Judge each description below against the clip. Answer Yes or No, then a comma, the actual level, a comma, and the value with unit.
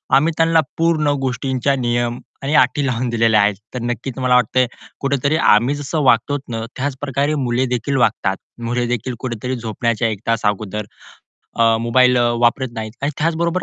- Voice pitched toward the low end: Yes, low, 125 Hz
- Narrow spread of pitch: No, average, 3.2 semitones